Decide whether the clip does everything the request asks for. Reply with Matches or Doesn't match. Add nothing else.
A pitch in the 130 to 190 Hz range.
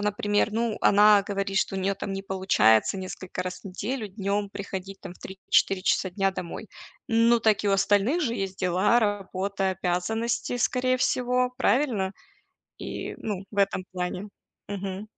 Doesn't match